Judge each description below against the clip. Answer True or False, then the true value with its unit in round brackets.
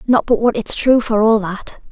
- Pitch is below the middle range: False (220 Hz)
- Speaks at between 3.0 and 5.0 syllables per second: True (4.7 syllables/s)